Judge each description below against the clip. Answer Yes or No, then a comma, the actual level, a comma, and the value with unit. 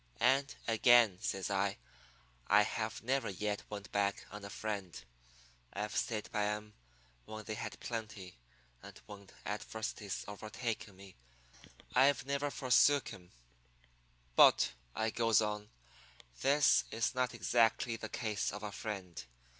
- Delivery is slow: Yes, slow, 130 wpm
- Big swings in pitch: No, narrow, 2.5 semitones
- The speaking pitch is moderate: No, low, 105 Hz